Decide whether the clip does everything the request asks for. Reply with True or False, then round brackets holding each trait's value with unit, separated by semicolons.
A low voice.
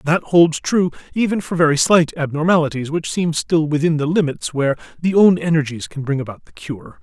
False (160 Hz)